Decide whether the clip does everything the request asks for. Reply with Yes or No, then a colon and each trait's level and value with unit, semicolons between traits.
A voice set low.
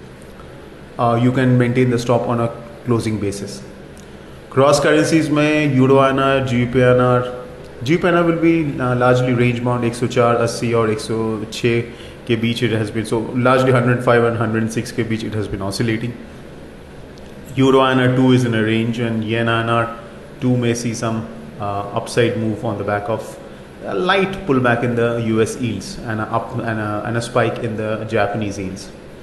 Yes: low, 115 Hz